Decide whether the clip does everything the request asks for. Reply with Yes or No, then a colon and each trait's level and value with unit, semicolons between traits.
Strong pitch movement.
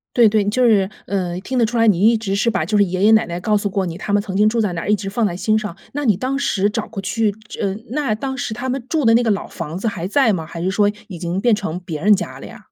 No: average, 3.2 semitones